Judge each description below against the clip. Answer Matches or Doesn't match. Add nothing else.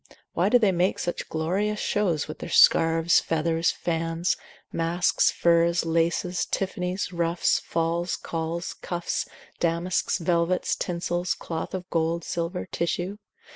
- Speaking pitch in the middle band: Matches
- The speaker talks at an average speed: Doesn't match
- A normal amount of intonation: Doesn't match